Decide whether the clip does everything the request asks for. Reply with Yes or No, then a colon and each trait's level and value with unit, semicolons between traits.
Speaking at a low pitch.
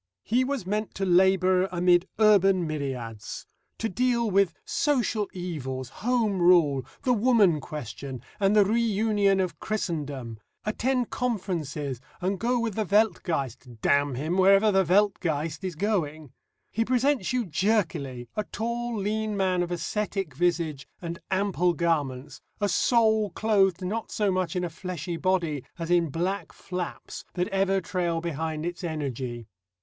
No: medium, 185 Hz